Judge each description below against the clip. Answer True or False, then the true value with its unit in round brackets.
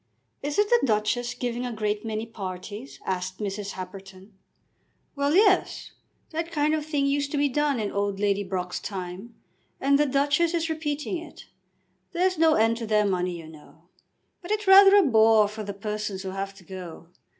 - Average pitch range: False (7.1 semitones)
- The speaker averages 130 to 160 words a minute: False (180 wpm)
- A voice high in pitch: True (220 Hz)